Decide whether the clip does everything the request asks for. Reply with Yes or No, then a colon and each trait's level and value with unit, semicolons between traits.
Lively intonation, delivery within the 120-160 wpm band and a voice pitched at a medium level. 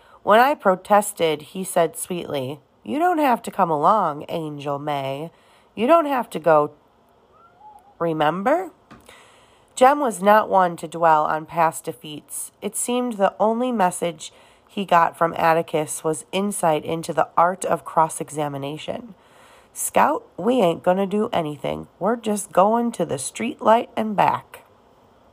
Yes: wide, 5.9 semitones; average, 145 wpm; medium, 180 Hz